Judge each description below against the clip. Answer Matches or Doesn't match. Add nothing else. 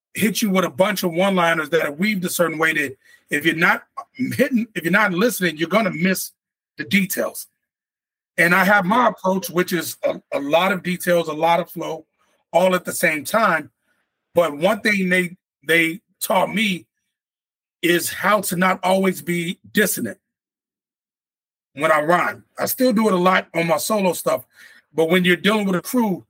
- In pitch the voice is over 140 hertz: Matches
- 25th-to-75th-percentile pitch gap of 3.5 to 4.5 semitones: Matches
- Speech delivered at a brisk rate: Doesn't match